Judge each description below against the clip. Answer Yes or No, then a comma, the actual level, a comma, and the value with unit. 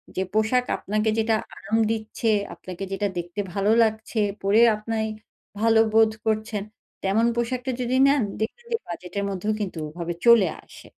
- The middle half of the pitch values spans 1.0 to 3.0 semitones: Yes, narrow, 2.5 semitones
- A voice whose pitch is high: Yes, high, 220 Hz